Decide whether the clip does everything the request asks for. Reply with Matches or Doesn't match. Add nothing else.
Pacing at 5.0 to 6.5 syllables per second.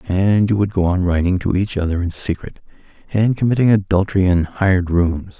Matches